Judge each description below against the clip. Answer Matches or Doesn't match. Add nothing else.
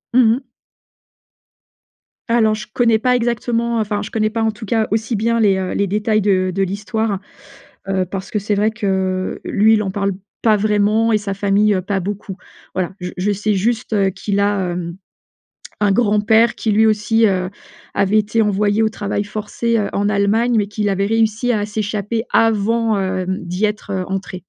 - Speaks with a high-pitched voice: Matches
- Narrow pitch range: Matches